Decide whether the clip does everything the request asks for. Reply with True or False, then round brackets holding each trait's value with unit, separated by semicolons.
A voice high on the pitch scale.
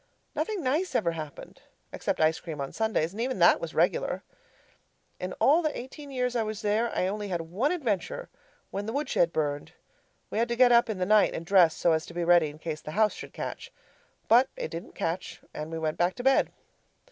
True (205 Hz)